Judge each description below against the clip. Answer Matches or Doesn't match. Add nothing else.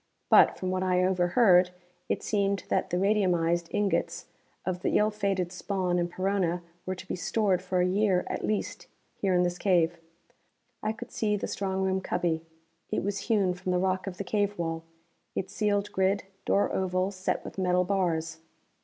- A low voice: Doesn't match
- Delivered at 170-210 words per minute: Matches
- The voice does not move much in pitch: Matches